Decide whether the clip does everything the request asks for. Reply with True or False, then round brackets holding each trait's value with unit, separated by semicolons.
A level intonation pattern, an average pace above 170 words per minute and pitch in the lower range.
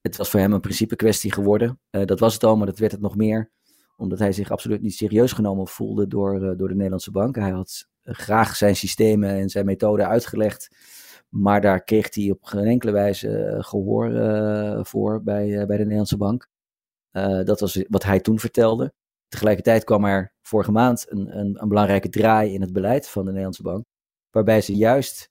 True (1.8 semitones; 200 wpm; 105 Hz)